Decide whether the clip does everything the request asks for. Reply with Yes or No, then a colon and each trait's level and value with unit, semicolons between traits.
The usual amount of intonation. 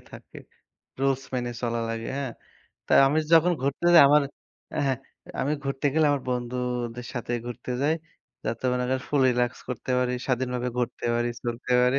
No: narrow, 2.1 semitones